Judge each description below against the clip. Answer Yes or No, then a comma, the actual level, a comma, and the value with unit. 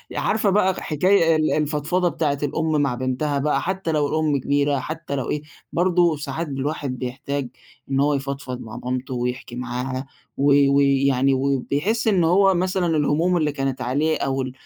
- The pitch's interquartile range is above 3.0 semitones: Yes, average, 3.4 semitones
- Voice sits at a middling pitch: Yes, medium, 145 Hz